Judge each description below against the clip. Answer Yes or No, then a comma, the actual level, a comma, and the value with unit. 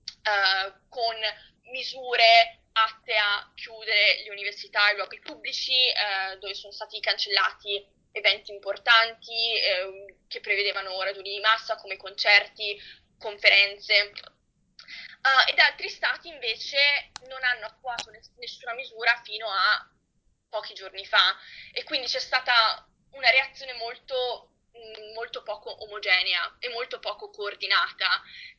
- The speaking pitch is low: No, high, 220 Hz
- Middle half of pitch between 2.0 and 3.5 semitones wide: No, average, 4.0 semitones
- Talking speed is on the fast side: No, average, 120 wpm